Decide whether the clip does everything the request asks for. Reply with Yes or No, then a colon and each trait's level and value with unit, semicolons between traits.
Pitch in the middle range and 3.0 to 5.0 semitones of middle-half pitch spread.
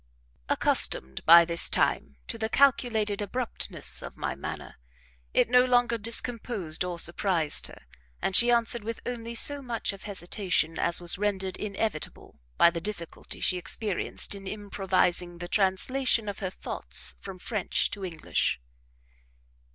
No: high, 200 Hz; average, 4.4 semitones